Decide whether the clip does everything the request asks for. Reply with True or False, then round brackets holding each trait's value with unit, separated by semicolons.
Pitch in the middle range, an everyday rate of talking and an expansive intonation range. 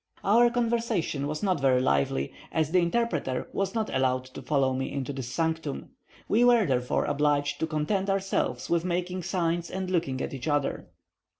True (160 Hz; 175 wpm; 5.8 semitones)